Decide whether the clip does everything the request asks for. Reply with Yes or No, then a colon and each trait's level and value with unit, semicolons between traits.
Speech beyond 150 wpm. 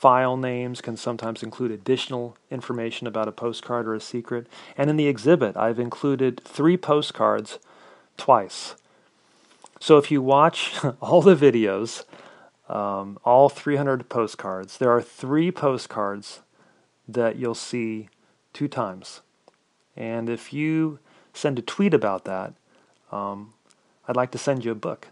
No: average, 140 wpm